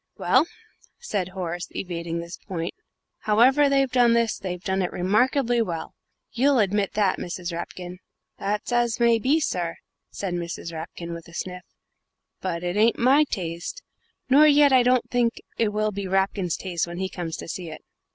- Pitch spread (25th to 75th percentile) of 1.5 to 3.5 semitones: No, wide, 5.5 semitones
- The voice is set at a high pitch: Yes, high, 195 Hz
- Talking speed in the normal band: Yes, average, 170 wpm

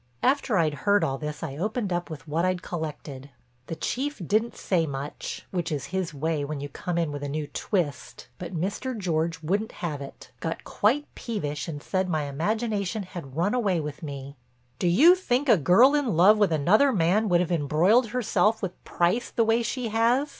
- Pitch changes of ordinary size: No, wide, 6.2 semitones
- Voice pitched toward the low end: No, medium, 180 Hz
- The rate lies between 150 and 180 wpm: No, average, 195 wpm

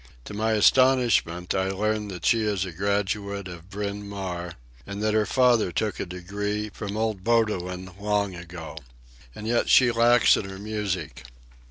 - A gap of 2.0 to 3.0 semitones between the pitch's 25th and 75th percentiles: Yes, average, 2.7 semitones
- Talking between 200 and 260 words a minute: No, average, 165 wpm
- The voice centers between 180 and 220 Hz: No, low, 100 Hz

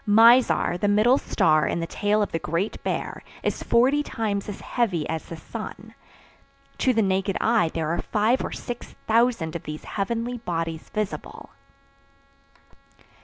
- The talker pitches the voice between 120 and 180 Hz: No, high, 205 Hz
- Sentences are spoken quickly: No, average, 155 wpm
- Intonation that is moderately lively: No, wide, 5.7 semitones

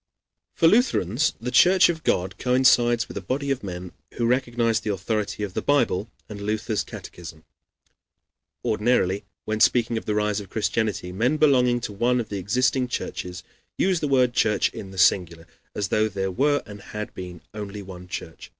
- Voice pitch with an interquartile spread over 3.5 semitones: Yes, average, 4.4 semitones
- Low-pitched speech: Yes, low, 110 Hz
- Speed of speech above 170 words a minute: Yes, average, 180 wpm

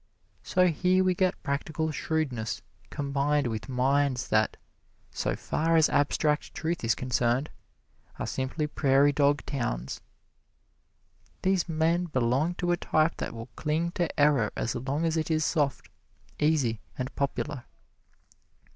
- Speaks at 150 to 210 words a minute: No, slow, 135 wpm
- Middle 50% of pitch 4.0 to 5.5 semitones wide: No, average, 3.6 semitones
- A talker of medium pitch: Yes, medium, 145 Hz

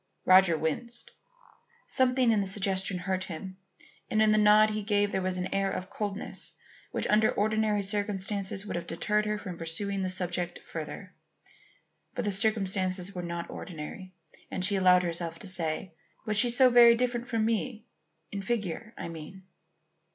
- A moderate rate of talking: Yes, average, 165 wpm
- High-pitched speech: Yes, high, 195 Hz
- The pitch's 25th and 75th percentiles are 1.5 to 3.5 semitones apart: Yes, average, 2.7 semitones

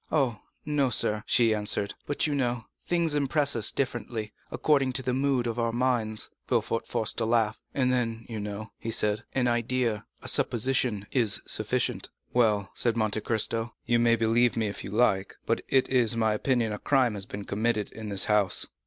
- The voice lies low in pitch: Yes, low, 115 Hz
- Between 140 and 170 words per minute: No, average, 190 wpm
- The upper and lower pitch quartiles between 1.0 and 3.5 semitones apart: Yes, average, 2.9 semitones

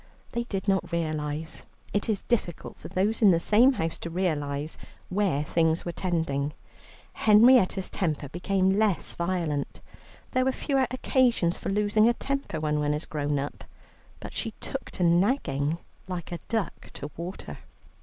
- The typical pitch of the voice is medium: Yes, medium, 175 Hz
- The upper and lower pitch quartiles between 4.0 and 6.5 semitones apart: Yes, average, 5.2 semitones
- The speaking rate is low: No, average, 155 wpm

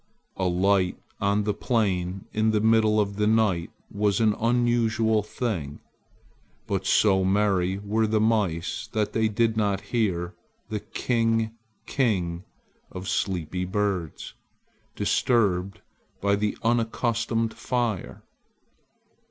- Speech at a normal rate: No, slow, 110 wpm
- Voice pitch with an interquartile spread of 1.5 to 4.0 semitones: Yes, average, 2.8 semitones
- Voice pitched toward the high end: No, low, 105 Hz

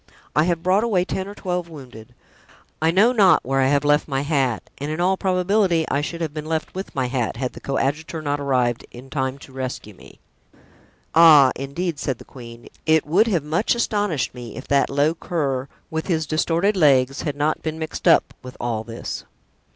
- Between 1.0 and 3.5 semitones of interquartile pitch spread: No, average, 4.4 semitones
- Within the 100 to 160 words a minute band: No, average, 200 wpm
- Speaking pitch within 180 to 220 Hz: No, medium, 150 Hz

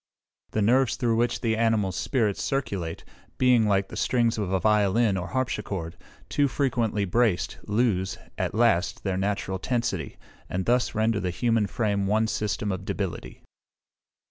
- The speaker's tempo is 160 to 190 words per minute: No, average, 150 wpm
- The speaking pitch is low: Yes, low, 105 Hz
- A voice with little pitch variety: No, average, 3.5 semitones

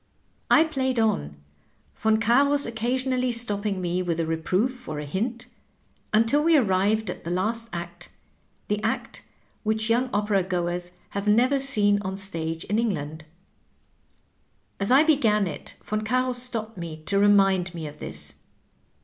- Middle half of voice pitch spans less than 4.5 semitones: No, average, 5.0 semitones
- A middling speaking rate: Yes, average, 150 wpm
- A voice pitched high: Yes, high, 210 Hz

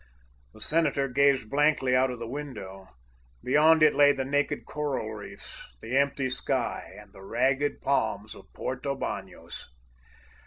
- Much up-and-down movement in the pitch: No, average, 3.3 semitones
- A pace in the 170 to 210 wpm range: No, average, 145 wpm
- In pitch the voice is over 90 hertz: Yes, low, 135 Hz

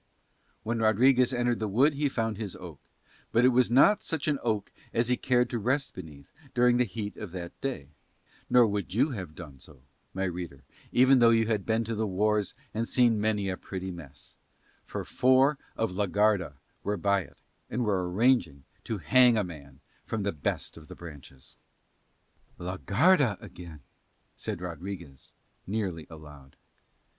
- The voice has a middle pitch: No, low, 105 Hz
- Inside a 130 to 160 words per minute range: No, average, 170 wpm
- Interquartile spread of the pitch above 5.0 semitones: Yes, wide, 5.5 semitones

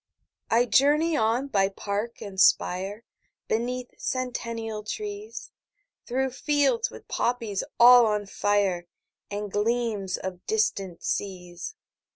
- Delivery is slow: Yes, slow, 115 wpm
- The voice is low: No, high, 225 Hz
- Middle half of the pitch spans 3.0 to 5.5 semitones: Yes, average, 3.9 semitones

